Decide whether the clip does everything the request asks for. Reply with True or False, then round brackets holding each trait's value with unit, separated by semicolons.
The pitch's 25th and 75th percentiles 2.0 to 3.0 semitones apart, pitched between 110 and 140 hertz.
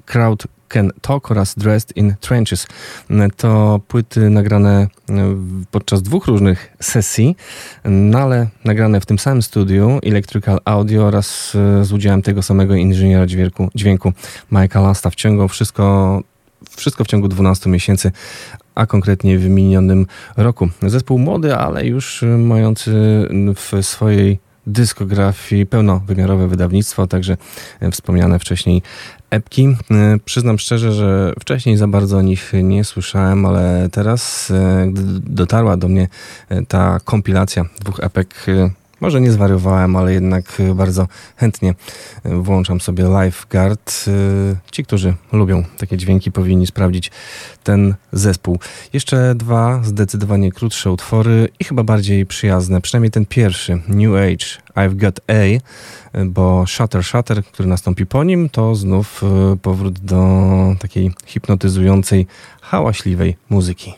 False (2.6 semitones; 100 Hz)